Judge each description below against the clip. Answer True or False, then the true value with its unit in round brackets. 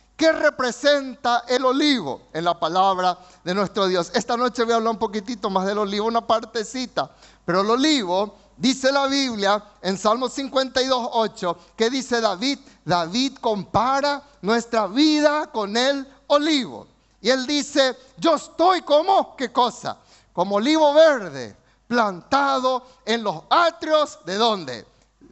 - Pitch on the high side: True (240 Hz)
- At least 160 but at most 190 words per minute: False (140 wpm)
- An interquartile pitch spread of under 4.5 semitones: False (5.2 semitones)